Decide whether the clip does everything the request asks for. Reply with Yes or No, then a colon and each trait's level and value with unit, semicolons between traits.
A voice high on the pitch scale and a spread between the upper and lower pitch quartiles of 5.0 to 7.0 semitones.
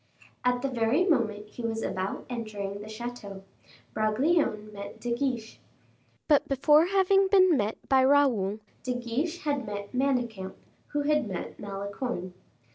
Yes: high, 240 Hz; wide, 5.4 semitones